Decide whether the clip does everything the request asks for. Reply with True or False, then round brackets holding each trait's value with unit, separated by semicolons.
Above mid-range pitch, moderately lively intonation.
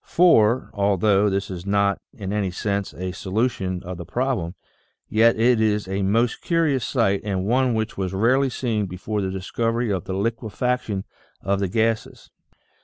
False (105 Hz; 3.3 semitones)